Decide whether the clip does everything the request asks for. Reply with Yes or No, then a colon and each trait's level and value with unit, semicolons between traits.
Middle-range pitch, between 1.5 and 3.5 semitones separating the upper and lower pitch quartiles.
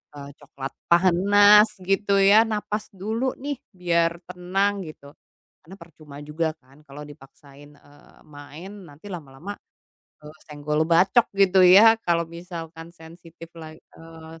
No: medium, 170 Hz; average, 4.4 semitones